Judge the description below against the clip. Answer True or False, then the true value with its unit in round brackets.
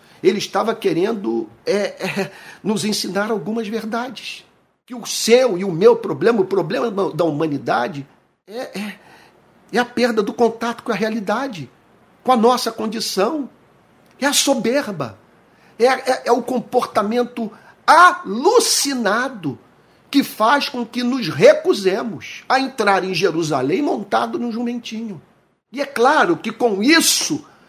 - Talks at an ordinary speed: True (135 wpm)